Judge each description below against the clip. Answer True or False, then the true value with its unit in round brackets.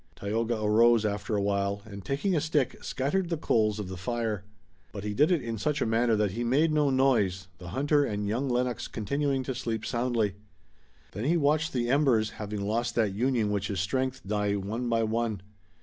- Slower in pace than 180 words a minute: False (200 wpm)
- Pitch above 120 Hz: False (115 Hz)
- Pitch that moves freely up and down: False (4.3 semitones)